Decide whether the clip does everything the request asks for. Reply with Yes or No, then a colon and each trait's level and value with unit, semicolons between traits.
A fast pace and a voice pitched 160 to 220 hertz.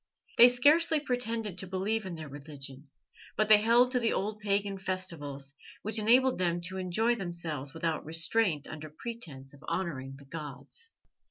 No: average, 160 wpm; medium, 185 Hz